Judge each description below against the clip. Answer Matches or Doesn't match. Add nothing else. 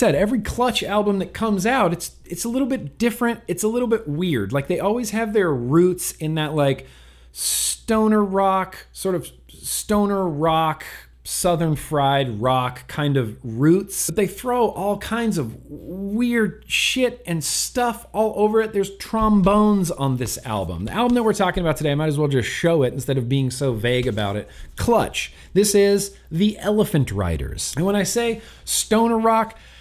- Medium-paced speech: Matches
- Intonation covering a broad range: Matches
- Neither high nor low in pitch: Matches